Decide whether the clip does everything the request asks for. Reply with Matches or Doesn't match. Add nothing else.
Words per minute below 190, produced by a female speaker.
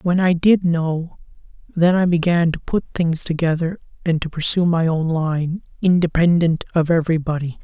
Doesn't match